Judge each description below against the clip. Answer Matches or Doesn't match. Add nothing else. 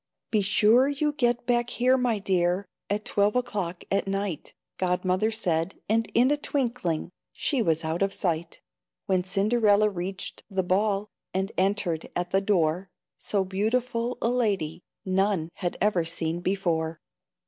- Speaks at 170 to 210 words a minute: Doesn't match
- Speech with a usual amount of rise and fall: Matches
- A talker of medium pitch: Doesn't match